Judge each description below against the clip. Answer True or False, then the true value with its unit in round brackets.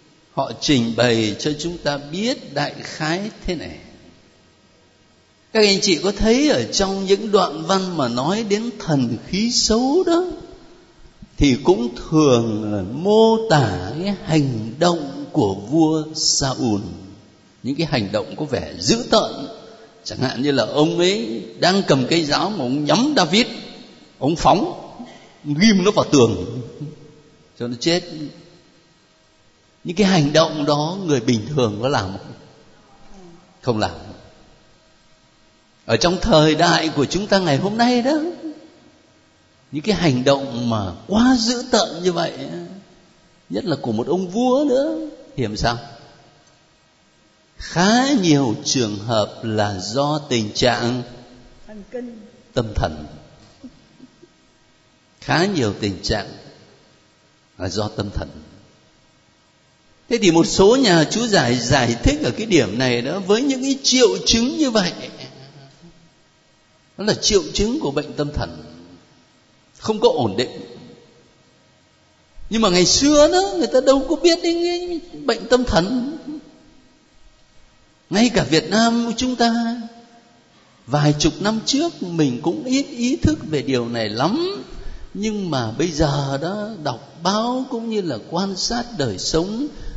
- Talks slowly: True (140 wpm)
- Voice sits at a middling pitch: True (165 Hz)